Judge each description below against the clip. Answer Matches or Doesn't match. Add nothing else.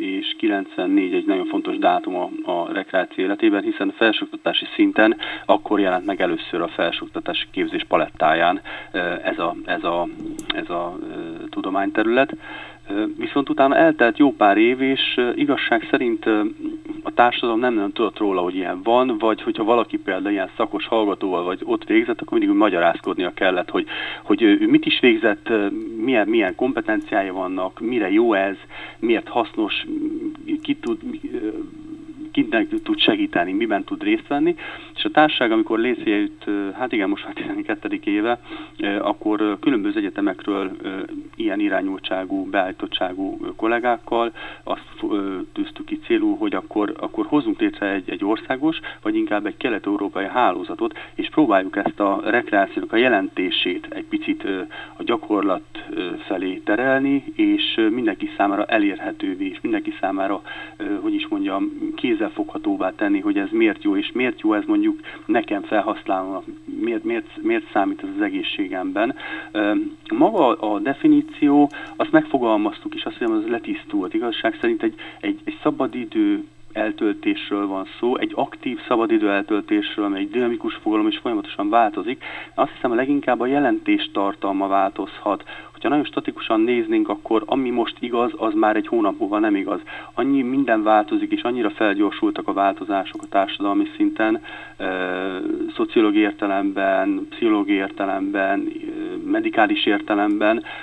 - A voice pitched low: Doesn't match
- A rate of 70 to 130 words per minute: Doesn't match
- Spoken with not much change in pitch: Matches